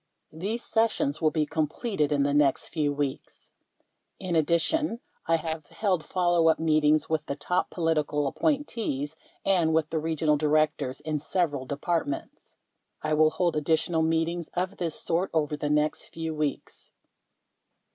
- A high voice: No, medium, 160 Hz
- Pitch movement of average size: No, narrow, 2.3 semitones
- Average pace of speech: Yes, average, 145 wpm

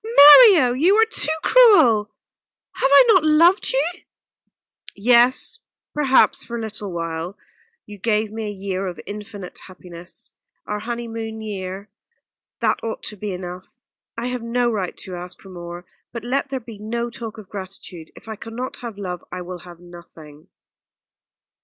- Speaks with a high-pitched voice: Yes, high, 215 Hz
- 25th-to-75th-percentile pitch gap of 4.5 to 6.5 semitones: Yes, average, 4.8 semitones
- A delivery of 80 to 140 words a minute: No, average, 160 wpm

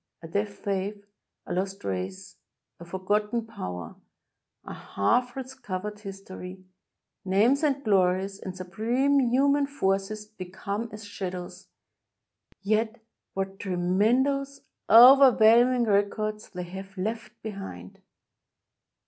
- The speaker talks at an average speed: No, slow, 125 wpm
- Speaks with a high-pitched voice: Yes, high, 205 Hz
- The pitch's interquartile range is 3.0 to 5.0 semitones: Yes, average, 3.7 semitones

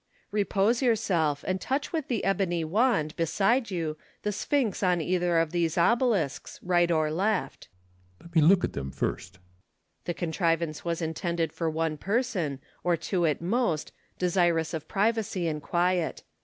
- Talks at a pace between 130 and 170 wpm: Yes, average, 160 wpm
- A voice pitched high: No, medium, 175 Hz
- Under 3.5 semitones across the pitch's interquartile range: No, average, 3.8 semitones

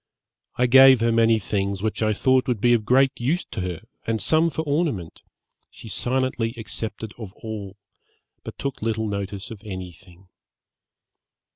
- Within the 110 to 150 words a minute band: No, average, 160 wpm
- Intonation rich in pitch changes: No, average, 4.2 semitones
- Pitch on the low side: Yes, low, 110 Hz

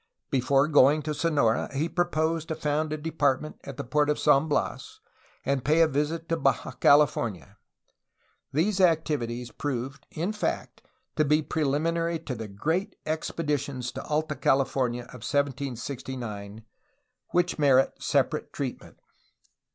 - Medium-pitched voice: Yes, medium, 145 Hz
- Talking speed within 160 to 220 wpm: No, average, 140 wpm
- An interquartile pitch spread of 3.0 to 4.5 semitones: Yes, average, 3.3 semitones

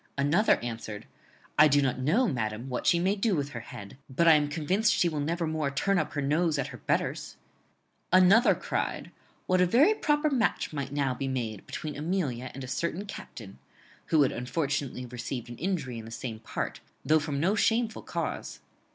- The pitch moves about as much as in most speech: No, wide, 6.1 semitones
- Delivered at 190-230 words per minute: Yes, average, 195 wpm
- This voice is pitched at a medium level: Yes, medium, 145 Hz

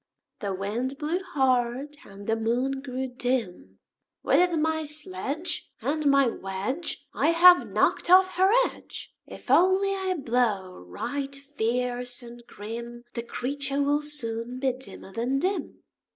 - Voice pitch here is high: Yes, very high, 260 Hz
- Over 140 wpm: No, slow, 135 wpm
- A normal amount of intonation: Yes, average, 4.3 semitones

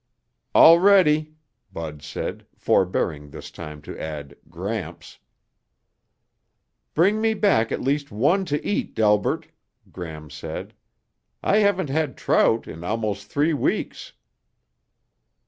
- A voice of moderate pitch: No, low, 115 Hz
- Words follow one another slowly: Yes, slow, 110 wpm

